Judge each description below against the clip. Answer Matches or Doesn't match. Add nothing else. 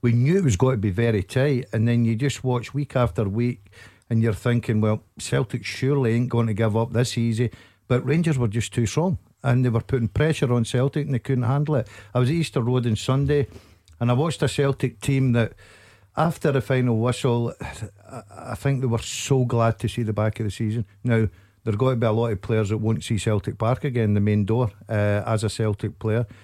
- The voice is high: Doesn't match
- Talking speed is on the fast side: Matches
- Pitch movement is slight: Doesn't match